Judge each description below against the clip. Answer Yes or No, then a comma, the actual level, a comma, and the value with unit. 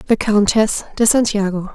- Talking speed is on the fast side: No, slow, 135 wpm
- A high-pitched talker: Yes, high, 210 Hz